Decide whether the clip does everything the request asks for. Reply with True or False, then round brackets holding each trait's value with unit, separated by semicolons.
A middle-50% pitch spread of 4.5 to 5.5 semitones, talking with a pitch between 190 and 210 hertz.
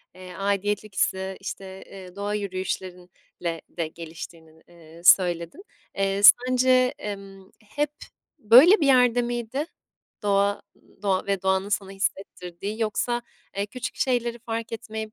False (3.7 semitones; 200 Hz)